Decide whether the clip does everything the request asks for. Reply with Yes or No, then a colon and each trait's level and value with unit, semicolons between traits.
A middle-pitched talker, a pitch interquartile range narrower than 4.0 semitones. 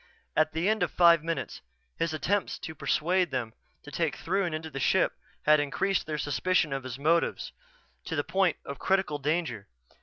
Yes: medium, 160 Hz; average, 3.4 semitones